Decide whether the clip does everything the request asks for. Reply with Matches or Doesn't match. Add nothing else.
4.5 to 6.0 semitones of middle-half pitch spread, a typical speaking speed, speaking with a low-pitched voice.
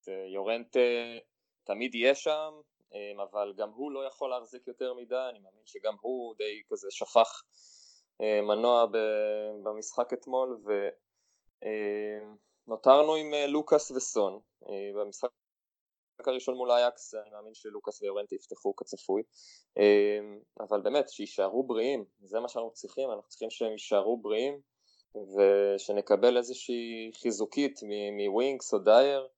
Matches